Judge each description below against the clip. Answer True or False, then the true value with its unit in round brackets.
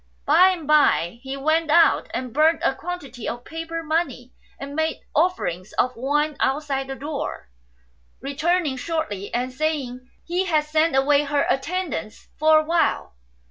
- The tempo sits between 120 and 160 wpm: True (155 wpm)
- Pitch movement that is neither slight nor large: True (3.4 semitones)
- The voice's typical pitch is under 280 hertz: False (295 Hz)